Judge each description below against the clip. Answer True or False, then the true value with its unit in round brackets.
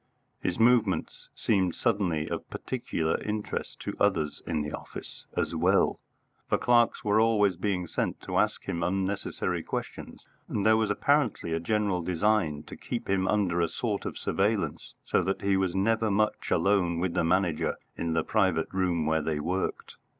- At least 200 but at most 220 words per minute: False (170 wpm)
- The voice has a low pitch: True (95 Hz)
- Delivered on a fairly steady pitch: False (4.0 semitones)